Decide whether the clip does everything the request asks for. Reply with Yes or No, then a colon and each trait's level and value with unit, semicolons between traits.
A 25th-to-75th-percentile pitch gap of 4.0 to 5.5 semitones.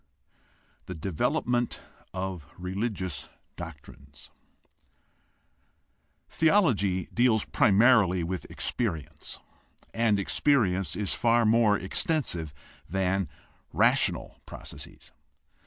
Yes: average, 4.6 semitones